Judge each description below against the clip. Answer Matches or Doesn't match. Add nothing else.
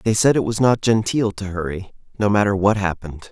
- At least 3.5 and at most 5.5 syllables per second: Doesn't match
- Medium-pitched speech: Doesn't match